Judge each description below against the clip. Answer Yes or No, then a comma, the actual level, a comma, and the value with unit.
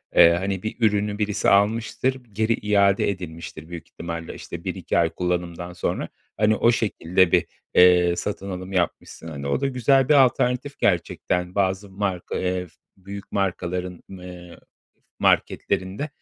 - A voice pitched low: Yes, very low, 95 Hz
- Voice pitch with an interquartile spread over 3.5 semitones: No, average, 2.9 semitones